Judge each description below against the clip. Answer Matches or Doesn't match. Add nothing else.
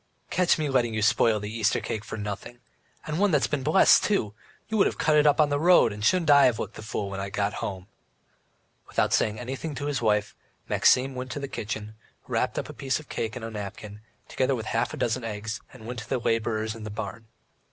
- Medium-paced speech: Doesn't match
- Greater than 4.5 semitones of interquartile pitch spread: Matches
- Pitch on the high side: Doesn't match